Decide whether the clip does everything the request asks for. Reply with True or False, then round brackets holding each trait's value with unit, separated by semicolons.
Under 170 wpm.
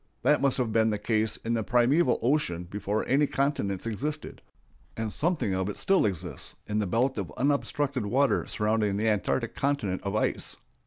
False (175 wpm)